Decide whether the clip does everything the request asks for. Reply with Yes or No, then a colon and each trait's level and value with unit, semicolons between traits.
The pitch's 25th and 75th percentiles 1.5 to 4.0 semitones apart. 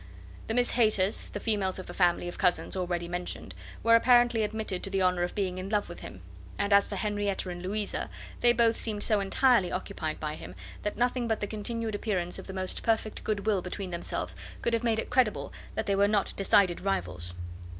Yes: average, 3.3 semitones